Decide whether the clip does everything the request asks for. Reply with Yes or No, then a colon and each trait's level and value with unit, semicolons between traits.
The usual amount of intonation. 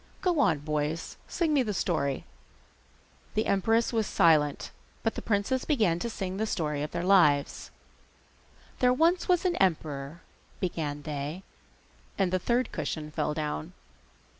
No: wide, 7.0 semitones